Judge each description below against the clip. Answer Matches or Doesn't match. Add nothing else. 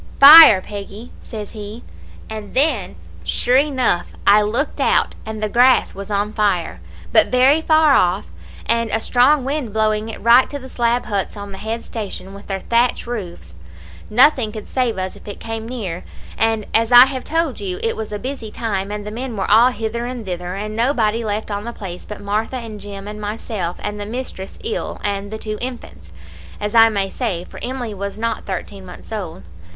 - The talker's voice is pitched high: Matches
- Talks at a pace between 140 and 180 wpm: Doesn't match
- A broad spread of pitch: Doesn't match